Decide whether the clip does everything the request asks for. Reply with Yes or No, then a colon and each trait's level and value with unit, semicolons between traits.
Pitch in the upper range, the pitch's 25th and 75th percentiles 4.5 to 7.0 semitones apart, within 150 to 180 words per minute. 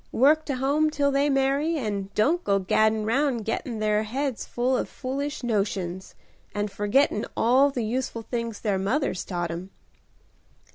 Yes: high, 235 Hz; average, 5.0 semitones; average, 155 wpm